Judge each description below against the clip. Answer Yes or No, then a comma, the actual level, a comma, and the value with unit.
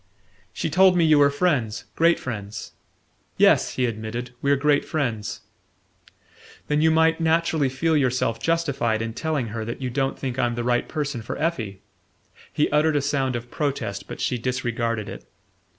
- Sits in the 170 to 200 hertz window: No, low, 130 Hz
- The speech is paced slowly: No, average, 165 wpm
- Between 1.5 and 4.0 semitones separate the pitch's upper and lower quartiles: No, average, 4.6 semitones